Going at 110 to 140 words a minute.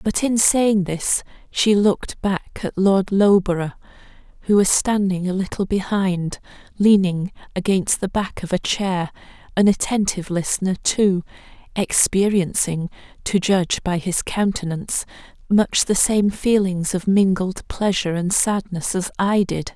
Yes: slow, 135 wpm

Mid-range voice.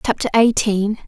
No: high, 215 Hz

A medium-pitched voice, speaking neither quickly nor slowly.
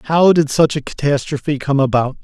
Yes: medium, 145 Hz; average, 190 wpm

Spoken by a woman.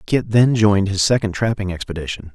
No: male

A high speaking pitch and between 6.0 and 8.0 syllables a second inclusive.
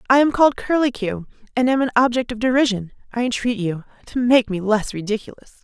Yes: high, 235 Hz; 6.1 syllables/s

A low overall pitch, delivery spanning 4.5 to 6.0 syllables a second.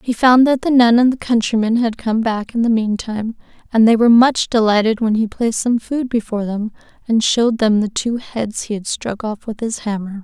No: high, 225 Hz; 5.4 syllables/s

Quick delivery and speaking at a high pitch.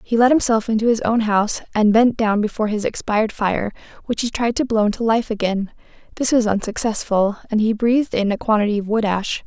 Yes: fast, 215 wpm; high, 220 Hz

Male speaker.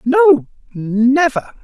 Yes: male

